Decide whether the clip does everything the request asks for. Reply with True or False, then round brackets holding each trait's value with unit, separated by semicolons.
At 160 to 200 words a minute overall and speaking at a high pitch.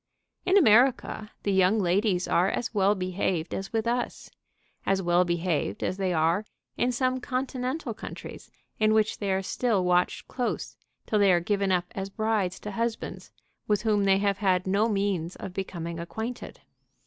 True (170 wpm; 195 Hz)